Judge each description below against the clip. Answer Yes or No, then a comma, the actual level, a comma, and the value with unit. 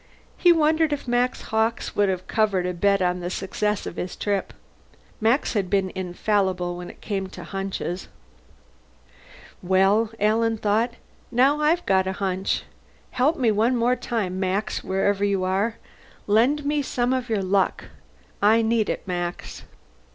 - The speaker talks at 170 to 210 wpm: No, average, 155 wpm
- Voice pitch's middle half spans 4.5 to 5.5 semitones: No, average, 3.9 semitones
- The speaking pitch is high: Yes, high, 205 Hz